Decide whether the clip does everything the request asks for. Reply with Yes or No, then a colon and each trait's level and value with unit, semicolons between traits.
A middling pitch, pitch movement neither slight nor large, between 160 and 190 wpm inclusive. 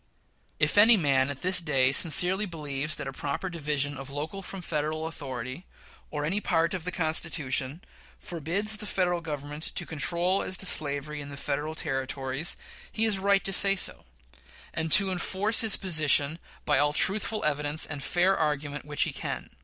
Yes: medium, 155 Hz; average, 4.3 semitones; average, 170 wpm